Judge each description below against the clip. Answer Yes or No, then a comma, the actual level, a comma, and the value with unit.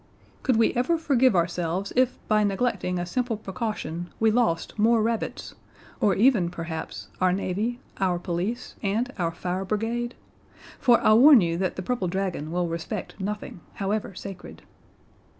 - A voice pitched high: Yes, high, 200 Hz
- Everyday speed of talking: Yes, average, 150 wpm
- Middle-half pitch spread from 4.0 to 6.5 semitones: Yes, average, 4.7 semitones